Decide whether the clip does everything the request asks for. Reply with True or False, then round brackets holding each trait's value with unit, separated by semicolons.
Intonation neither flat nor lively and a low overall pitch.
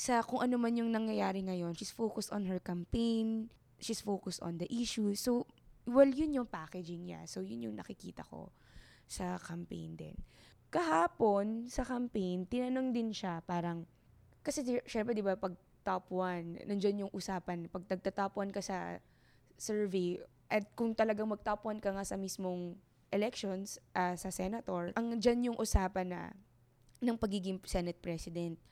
False (4.1 semitones; 195 Hz)